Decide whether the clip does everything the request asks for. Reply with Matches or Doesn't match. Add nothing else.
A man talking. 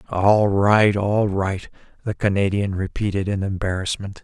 Matches